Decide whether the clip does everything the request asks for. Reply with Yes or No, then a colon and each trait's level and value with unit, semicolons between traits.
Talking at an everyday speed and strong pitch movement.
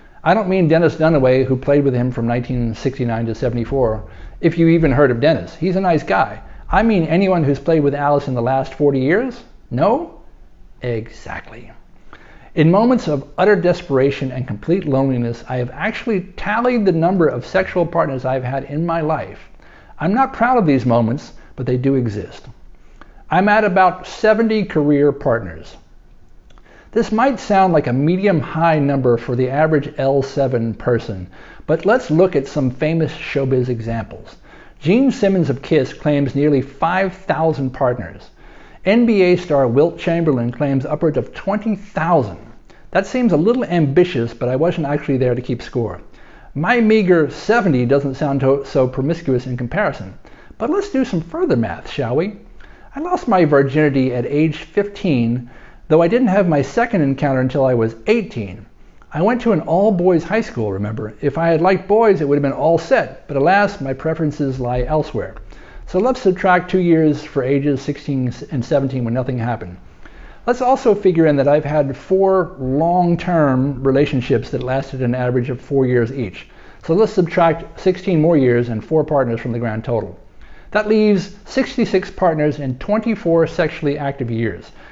Yes: average, 170 wpm; wide, 6.1 semitones